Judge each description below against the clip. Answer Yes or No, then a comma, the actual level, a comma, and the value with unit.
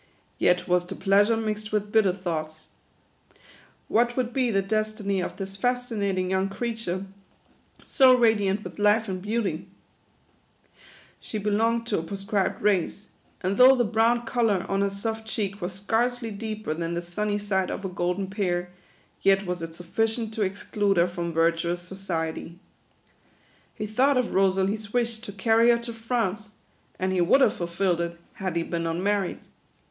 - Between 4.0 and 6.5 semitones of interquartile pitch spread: No, average, 3.5 semitones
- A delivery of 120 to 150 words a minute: No, average, 165 wpm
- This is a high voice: Yes, high, 200 Hz